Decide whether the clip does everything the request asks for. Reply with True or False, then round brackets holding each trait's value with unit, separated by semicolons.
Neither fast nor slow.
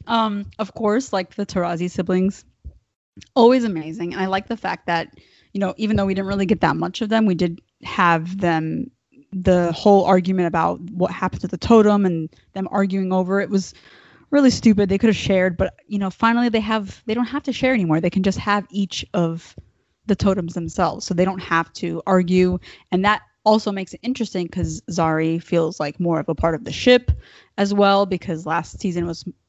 False (210 wpm)